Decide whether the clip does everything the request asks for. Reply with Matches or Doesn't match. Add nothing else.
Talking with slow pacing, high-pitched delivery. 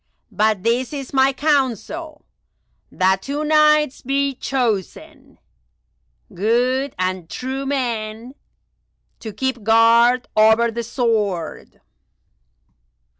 Matches